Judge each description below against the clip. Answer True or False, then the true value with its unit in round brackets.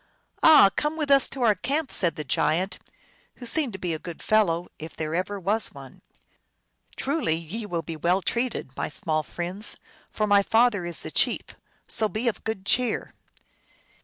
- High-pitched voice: True (200 Hz)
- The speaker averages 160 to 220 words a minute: True (185 wpm)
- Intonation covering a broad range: True (5.7 semitones)